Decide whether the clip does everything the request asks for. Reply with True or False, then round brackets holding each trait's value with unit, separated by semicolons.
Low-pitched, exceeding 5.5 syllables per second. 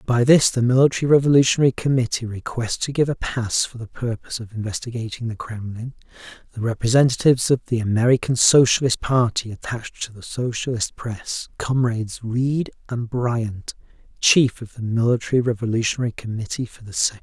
True (120 Hz; 5.8 syllables/s)